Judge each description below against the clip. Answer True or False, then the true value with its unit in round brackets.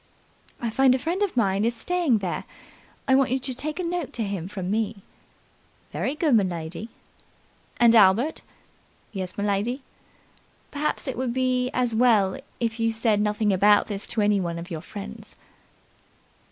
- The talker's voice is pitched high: True (225 Hz)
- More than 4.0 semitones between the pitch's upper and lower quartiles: True (4.5 semitones)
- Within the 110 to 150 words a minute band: False (165 wpm)